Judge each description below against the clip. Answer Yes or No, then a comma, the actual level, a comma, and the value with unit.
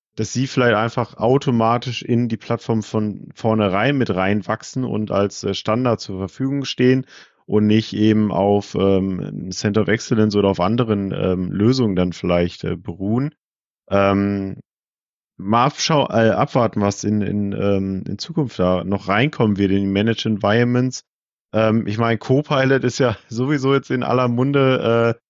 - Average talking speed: Yes, average, 155 wpm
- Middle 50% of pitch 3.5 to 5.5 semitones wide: Yes, average, 3.9 semitones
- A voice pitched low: Yes, low, 110 Hz